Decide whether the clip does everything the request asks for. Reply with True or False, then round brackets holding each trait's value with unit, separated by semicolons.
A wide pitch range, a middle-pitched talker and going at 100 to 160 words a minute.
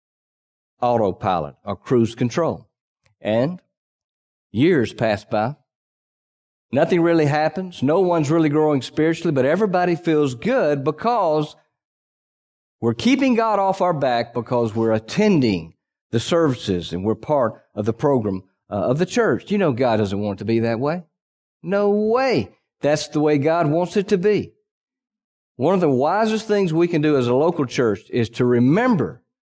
True (7.9 semitones; 155 Hz; 155 wpm)